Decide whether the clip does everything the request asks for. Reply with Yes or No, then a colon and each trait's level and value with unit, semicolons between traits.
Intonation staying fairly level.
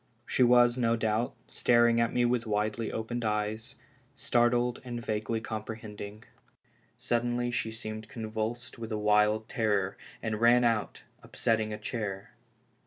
Yes: narrow, 1.9 semitones